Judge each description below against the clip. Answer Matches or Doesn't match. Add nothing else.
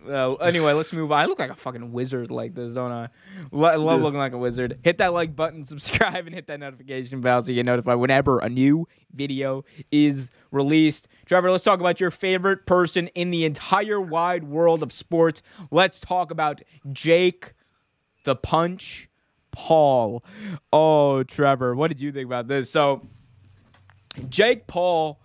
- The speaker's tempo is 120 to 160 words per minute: Doesn't match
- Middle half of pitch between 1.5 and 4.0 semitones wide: Doesn't match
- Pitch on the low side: Doesn't match